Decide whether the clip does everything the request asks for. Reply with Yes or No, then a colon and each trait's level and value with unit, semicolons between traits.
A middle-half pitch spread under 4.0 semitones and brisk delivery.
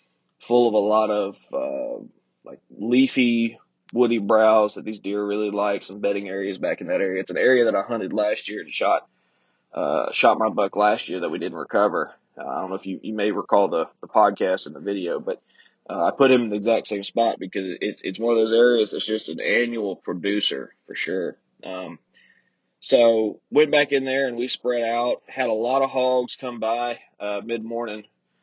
Yes: average, 2.9 semitones; fast, 210 wpm